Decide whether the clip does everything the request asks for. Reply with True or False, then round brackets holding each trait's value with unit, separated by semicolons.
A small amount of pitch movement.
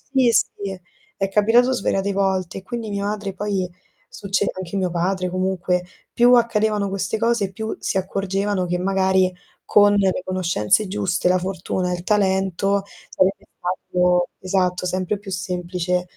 True (1.8 semitones)